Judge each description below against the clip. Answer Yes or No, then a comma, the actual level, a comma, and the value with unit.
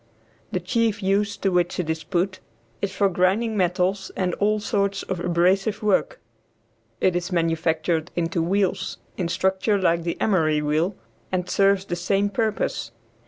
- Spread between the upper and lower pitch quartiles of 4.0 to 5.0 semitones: No, narrow, 2.6 semitones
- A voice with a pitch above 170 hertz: Yes, medium, 185 Hz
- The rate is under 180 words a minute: Yes, average, 155 wpm